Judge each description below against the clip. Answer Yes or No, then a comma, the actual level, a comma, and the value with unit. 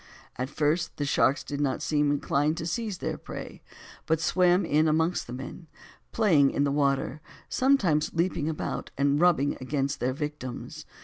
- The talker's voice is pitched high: No, medium, 150 Hz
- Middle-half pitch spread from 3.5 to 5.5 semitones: No, average, 3.0 semitones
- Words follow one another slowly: No, average, 165 wpm